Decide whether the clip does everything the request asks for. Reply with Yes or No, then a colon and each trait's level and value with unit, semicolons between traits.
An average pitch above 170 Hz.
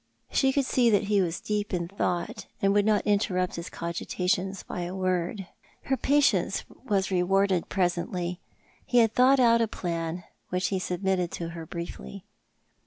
Yes: high, 190 Hz